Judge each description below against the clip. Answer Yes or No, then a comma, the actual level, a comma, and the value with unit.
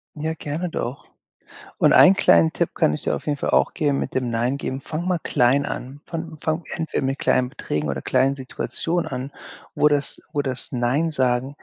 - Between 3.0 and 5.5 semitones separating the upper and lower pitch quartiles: Yes, average, 3.7 semitones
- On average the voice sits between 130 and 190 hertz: Yes, medium, 140 Hz